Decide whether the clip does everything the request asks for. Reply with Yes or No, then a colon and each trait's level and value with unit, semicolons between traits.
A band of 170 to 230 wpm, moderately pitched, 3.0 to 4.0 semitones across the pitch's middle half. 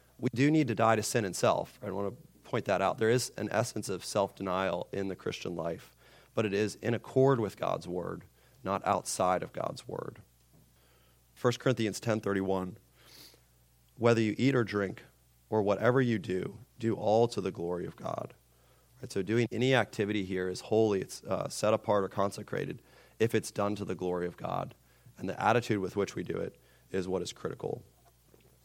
No: average, 195 wpm; low, 105 Hz; average, 3.6 semitones